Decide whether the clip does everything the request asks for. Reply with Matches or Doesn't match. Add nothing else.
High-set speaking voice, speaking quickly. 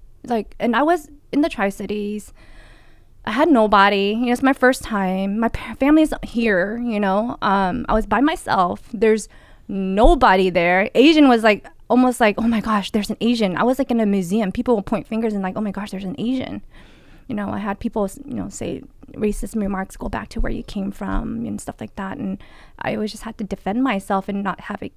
Matches